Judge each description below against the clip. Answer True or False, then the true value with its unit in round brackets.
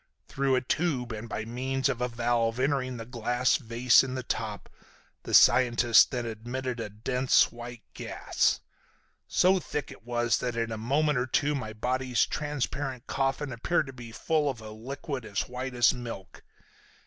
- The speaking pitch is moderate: False (125 Hz)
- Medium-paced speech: True (170 wpm)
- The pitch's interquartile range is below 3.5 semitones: True (2.4 semitones)